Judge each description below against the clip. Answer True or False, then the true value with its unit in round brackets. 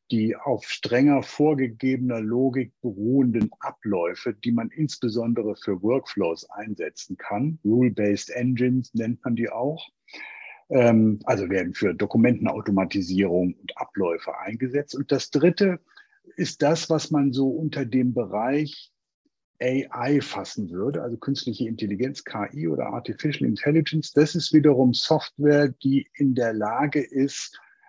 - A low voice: True (130 Hz)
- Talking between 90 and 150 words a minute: True (125 wpm)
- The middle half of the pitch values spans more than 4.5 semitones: False (4.1 semitones)